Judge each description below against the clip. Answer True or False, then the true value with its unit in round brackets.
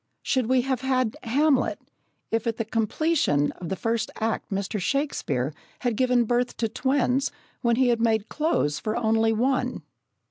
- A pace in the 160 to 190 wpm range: True (165 wpm)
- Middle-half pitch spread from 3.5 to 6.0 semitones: False (3.0 semitones)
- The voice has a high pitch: True (235 Hz)